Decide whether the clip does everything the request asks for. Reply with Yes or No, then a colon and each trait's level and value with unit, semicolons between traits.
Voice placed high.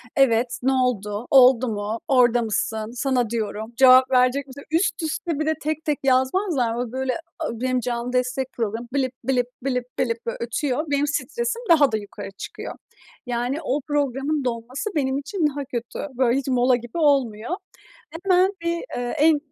Yes: very high, 255 Hz